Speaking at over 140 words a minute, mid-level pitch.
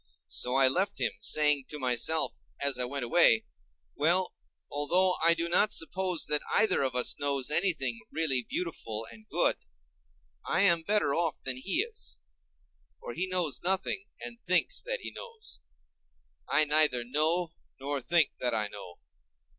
Yes: average, 155 wpm; medium, 155 Hz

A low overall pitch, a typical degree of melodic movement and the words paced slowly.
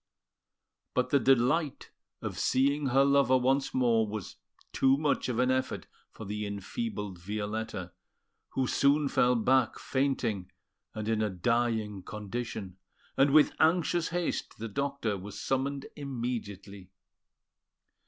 Yes: low, 125 Hz; average, 4.7 semitones; slow, 125 wpm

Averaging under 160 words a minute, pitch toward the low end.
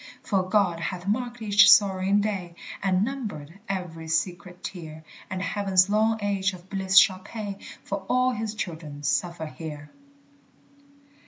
No: average, 140 wpm; high, 190 Hz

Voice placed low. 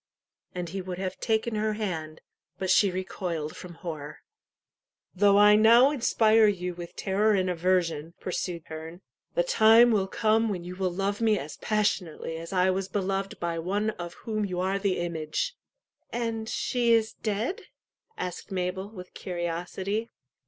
No: high, 190 Hz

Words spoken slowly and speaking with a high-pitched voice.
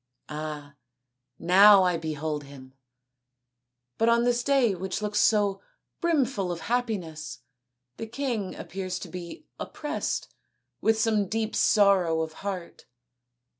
Yes: slow, 120 wpm; high, 195 Hz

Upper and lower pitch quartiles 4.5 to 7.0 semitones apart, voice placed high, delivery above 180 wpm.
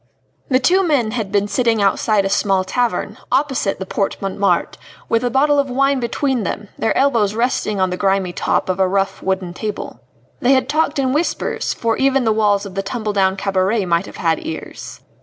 Yes: average, 4.8 semitones; high, 215 Hz; average, 200 wpm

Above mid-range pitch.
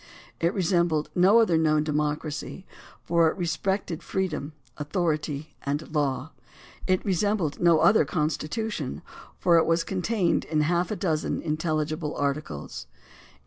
No: medium, 160 Hz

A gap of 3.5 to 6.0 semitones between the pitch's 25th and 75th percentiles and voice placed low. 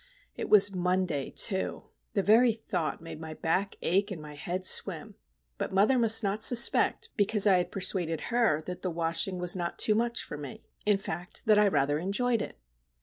No: average, 4.1 semitones; high, 190 Hz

